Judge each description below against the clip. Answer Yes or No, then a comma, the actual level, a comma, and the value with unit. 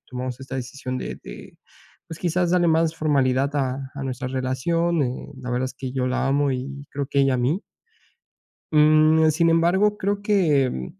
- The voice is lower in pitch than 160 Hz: Yes, medium, 140 Hz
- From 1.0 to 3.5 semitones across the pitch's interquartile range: No, average, 4.1 semitones